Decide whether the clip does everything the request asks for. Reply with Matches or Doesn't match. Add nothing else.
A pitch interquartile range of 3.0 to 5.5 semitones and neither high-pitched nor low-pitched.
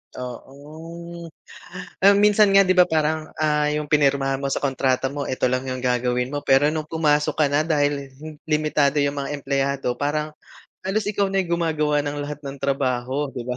Doesn't match